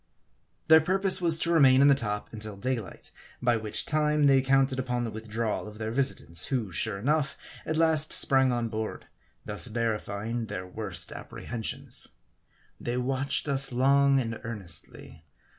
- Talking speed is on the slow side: No, average, 155 wpm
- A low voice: Yes, low, 125 Hz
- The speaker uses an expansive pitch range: No, average, 4.2 semitones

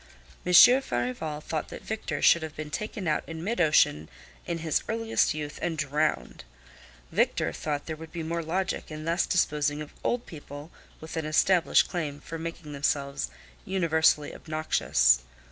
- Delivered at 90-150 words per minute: No, average, 160 wpm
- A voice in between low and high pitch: Yes, medium, 155 Hz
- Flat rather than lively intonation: Yes, narrow, 2.3 semitones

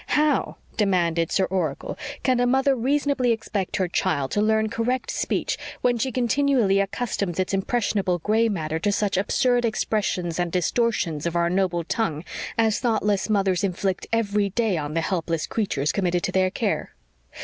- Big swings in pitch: No, average, 4.5 semitones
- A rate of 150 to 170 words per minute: Yes, average, 160 wpm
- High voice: Yes, high, 200 Hz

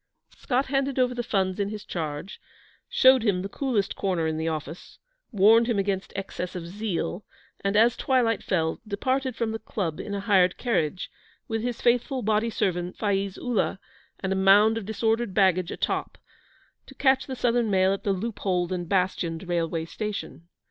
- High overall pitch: Yes, high, 200 Hz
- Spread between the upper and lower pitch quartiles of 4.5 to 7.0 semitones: No, average, 4.0 semitones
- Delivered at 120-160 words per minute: No, average, 175 wpm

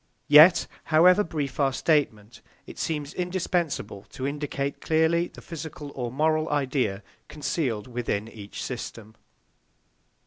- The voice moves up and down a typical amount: Yes, average, 4.7 semitones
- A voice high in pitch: No, medium, 145 Hz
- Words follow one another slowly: Yes, slow, 115 wpm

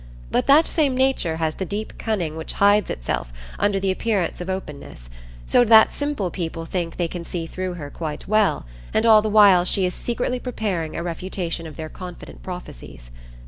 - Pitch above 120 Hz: Yes, medium, 185 Hz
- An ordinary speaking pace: Yes, average, 185 wpm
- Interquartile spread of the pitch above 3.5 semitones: Yes, average, 4.6 semitones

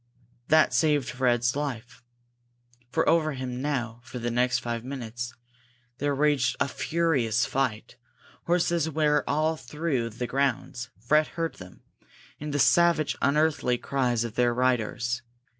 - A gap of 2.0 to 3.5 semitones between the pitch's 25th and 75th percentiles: No, average, 3.9 semitones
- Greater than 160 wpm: No, slow, 135 wpm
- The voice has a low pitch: Yes, low, 130 Hz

